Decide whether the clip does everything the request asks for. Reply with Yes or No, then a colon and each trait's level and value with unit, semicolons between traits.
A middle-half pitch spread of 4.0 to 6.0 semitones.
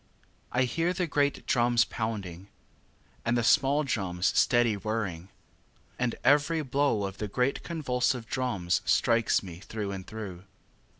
Yes: average, 5.2 semitones